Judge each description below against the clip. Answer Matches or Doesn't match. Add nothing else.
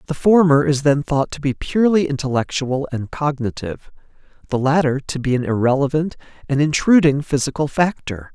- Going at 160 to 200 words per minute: Doesn't match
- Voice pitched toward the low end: Doesn't match